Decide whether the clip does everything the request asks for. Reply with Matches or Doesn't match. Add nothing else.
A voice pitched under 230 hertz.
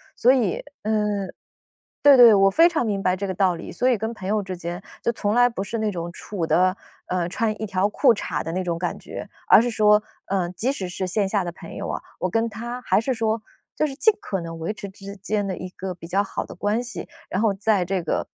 Matches